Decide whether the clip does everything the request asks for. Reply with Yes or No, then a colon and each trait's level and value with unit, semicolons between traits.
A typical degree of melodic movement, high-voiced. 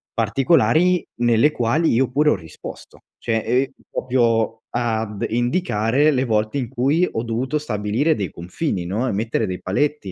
No: average, 4.4 semitones; low, 120 Hz